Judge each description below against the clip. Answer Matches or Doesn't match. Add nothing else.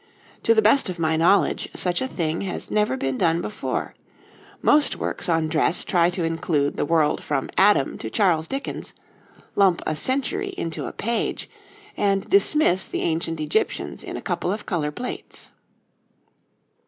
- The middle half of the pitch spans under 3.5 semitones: Doesn't match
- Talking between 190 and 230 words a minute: Doesn't match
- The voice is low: Doesn't match